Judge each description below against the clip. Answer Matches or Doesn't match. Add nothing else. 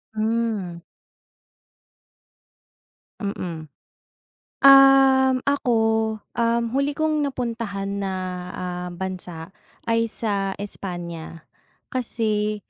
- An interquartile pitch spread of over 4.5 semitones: Matches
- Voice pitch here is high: Matches